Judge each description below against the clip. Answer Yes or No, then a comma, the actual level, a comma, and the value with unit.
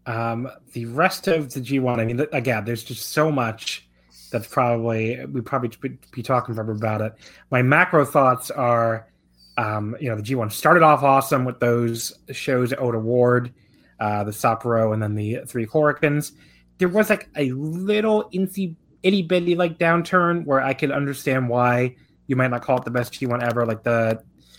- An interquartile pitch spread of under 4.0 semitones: No, average, 4.3 semitones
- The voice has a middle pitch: No, low, 125 Hz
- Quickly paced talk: No, average, 180 wpm